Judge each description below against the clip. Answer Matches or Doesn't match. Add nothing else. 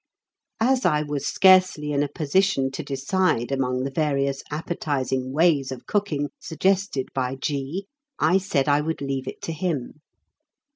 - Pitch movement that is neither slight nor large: Matches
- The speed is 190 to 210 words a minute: Doesn't match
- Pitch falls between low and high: Matches